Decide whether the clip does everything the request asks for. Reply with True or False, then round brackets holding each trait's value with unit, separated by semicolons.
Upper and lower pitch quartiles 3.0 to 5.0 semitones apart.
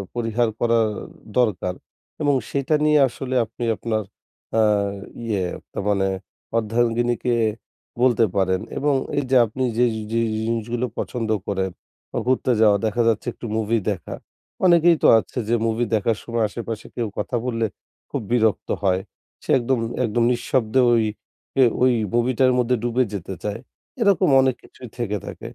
False (2.6 semitones)